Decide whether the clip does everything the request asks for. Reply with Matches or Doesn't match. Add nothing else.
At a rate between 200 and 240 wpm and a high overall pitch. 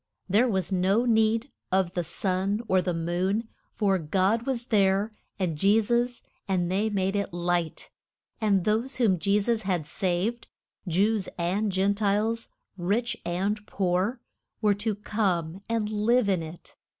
Doesn't match